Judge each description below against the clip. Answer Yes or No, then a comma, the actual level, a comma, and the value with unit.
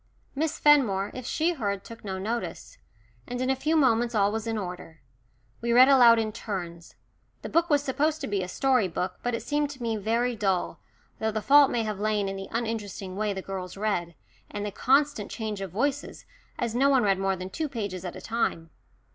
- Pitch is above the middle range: Yes, high, 220 Hz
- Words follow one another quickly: Yes, fast, 215 wpm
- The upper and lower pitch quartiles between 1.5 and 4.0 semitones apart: No, average, 4.9 semitones